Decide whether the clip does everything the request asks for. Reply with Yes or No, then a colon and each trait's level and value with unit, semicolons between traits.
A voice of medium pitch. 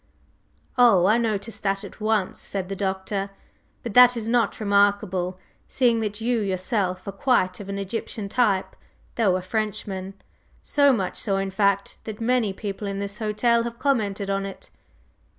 No: high, 205 Hz